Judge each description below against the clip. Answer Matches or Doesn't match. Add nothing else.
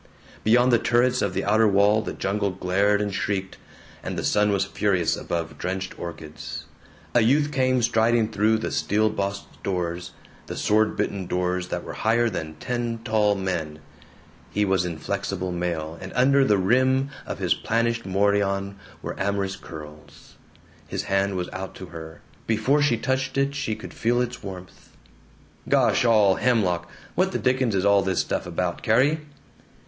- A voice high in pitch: Doesn't match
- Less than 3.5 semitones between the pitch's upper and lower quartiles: Doesn't match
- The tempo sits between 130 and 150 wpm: Doesn't match